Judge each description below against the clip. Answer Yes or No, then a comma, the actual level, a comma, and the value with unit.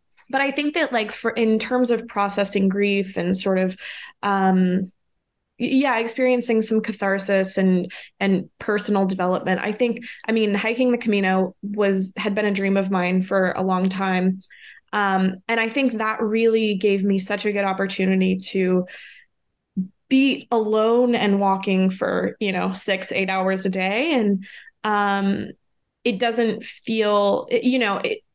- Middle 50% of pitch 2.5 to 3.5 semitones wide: Yes, average, 3.0 semitones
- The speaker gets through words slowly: No, average, 155 wpm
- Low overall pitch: No, high, 200 Hz